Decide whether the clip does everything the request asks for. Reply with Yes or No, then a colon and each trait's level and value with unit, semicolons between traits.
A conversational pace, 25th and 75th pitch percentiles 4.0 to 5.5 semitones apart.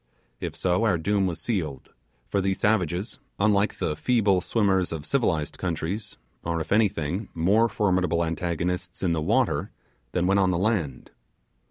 No: average, 155 wpm; average, 3.4 semitones